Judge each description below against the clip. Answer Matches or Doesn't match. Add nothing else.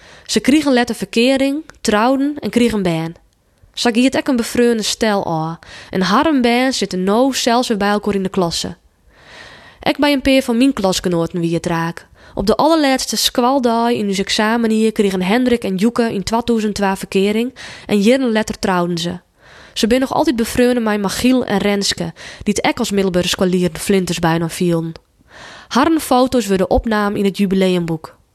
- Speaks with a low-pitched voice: Doesn't match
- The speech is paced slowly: Doesn't match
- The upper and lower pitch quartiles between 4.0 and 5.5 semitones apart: Matches